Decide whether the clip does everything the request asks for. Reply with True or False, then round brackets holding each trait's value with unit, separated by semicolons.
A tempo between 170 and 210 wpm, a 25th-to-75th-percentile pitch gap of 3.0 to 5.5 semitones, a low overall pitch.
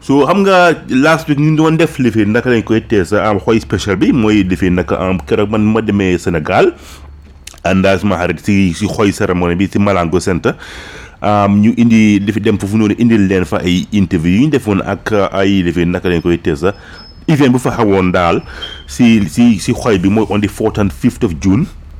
True (200 wpm; 3.9 semitones; 100 Hz)